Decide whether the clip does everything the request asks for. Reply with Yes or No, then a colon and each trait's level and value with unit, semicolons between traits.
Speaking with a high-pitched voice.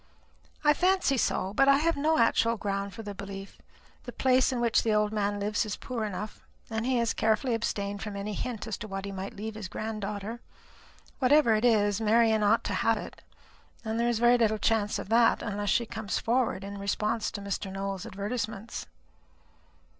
Yes: high, 220 Hz